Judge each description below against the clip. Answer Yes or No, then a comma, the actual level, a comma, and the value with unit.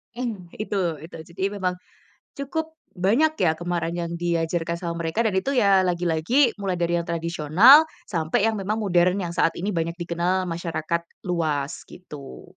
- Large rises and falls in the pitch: No, average, 3.1 semitones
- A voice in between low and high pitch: Yes, medium, 175 Hz